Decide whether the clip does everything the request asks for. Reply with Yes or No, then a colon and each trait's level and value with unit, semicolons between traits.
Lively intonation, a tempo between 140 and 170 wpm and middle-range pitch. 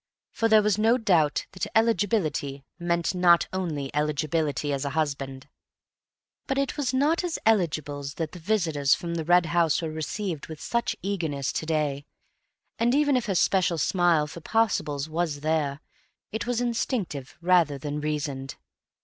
Yes: wide, 5.8 semitones; average, 160 wpm; medium, 165 Hz